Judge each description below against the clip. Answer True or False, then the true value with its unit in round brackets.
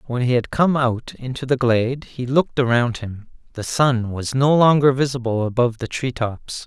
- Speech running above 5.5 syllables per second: False (5.0 syllables/s)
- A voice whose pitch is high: False (125 Hz)